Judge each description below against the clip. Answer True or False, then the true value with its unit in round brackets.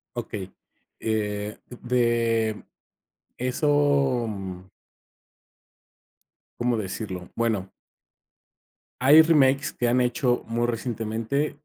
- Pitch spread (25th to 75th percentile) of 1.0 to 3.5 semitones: True (3.0 semitones)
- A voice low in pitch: True (120 Hz)